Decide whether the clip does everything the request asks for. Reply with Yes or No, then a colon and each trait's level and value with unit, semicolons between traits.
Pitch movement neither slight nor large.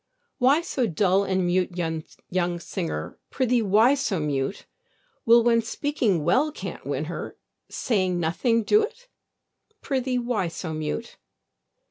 No: wide, 6.3 semitones